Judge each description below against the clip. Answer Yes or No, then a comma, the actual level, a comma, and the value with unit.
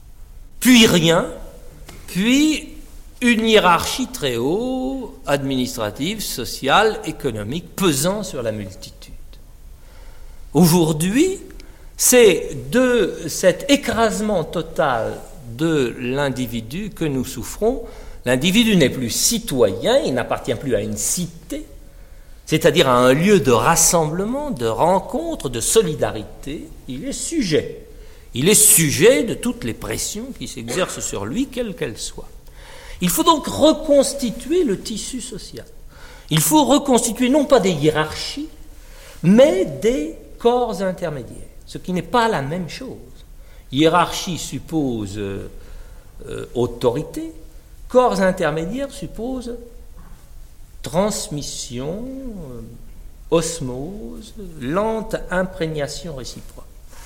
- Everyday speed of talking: No, slow, 105 wpm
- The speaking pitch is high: No, medium, 170 Hz